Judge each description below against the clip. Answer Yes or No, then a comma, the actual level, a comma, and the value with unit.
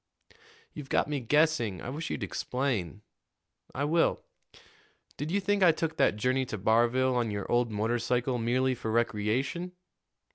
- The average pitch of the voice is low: Yes, low, 125 Hz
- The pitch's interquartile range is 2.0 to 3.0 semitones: No, average, 4.7 semitones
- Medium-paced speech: Yes, average, 150 wpm